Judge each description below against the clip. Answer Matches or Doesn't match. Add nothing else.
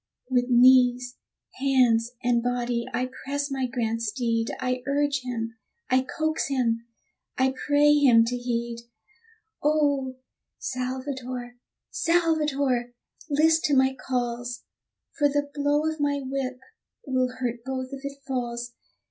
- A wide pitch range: Doesn't match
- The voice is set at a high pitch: Matches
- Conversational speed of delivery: Doesn't match